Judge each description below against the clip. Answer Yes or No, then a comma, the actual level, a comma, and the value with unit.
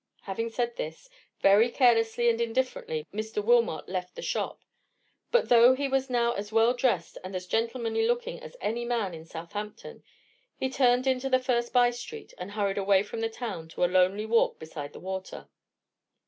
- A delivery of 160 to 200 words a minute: Yes, average, 180 wpm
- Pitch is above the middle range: Yes, high, 230 Hz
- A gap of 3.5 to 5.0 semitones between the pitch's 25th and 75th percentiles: Yes, average, 4.1 semitones